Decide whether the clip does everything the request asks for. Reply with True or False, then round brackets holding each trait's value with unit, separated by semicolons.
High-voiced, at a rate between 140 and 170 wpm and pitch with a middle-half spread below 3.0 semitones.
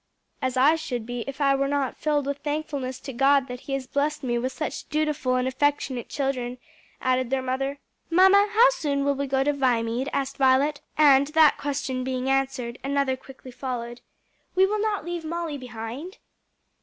False (275 Hz; 180 wpm; 2.4 semitones)